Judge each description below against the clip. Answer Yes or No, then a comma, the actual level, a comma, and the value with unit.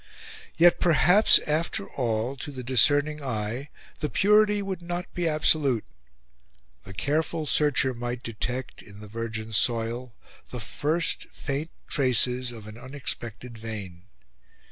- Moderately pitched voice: No, low, 130 Hz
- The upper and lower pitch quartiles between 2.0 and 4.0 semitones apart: No, average, 5.1 semitones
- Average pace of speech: No, slow, 125 wpm